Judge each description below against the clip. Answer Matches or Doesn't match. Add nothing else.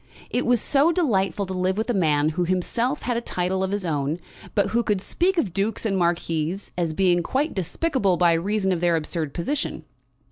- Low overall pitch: Doesn't match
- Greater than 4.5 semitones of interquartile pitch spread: Matches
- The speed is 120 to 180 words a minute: Doesn't match